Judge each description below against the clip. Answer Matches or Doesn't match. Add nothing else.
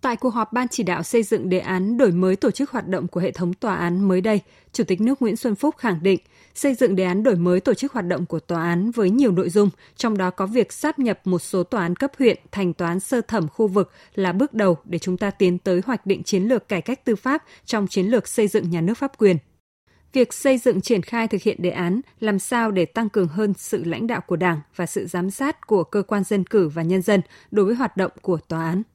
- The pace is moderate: Doesn't match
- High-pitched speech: Matches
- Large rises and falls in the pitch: Doesn't match